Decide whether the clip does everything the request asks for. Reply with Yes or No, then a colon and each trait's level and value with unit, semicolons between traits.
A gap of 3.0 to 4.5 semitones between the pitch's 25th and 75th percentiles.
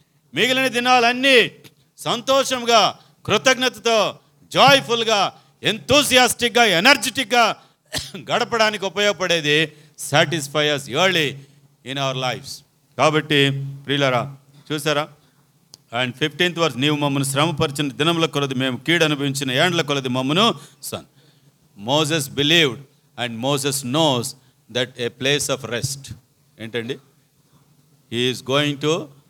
Yes: average, 3.8 semitones